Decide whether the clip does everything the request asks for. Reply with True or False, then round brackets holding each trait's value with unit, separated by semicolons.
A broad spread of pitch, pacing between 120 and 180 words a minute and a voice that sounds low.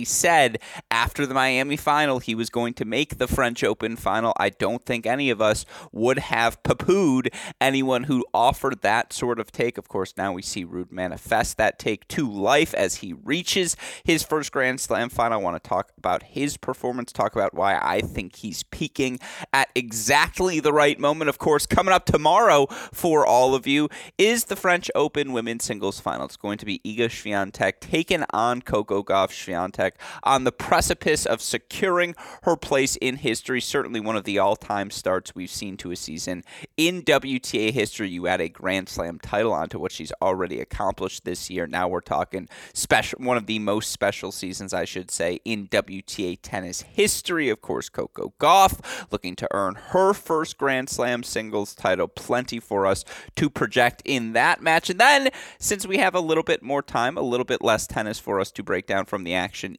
False (6.2 semitones; 195 wpm; 125 Hz)